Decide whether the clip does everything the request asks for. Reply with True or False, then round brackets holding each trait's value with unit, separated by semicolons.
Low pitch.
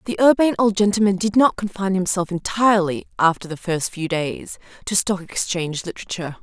False (190 Hz)